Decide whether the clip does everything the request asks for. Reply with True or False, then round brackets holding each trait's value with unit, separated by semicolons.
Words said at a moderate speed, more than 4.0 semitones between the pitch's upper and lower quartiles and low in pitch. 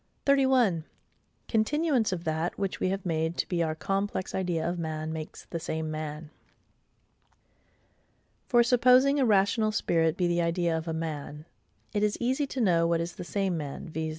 False (170 wpm; 4.6 semitones; 175 Hz)